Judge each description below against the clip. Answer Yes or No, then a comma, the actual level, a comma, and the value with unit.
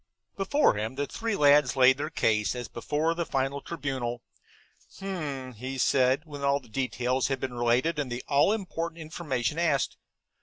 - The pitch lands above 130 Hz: Yes, medium, 140 Hz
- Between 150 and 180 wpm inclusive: Yes, average, 165 wpm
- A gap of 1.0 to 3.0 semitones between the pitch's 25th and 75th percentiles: No, average, 4.1 semitones